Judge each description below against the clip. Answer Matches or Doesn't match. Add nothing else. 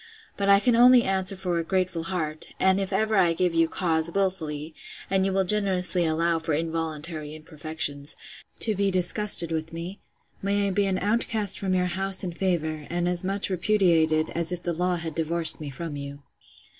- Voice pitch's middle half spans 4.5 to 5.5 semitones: Doesn't match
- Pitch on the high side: Doesn't match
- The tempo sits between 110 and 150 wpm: Doesn't match